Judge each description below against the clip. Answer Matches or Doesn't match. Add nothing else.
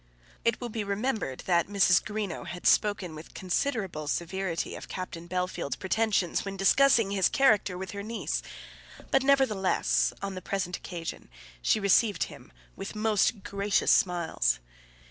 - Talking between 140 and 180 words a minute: Matches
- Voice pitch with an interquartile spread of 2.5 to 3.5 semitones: Matches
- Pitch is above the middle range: Matches